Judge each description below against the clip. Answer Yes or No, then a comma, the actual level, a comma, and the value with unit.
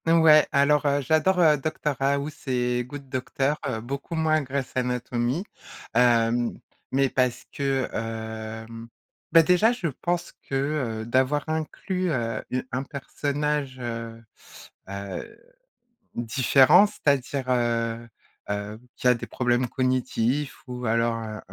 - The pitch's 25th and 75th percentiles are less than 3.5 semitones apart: No, average, 4.0 semitones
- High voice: No, low, 130 Hz